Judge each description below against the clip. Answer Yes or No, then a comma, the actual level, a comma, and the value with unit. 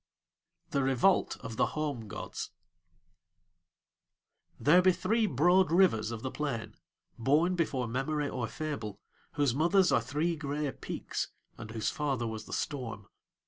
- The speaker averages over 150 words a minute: No, average, 140 wpm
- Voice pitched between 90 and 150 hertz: Yes, medium, 140 Hz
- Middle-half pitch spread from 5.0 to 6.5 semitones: Yes, wide, 5.6 semitones